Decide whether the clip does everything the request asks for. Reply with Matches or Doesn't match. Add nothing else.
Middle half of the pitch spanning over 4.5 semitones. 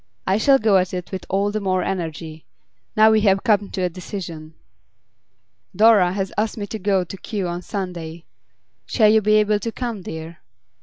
Doesn't match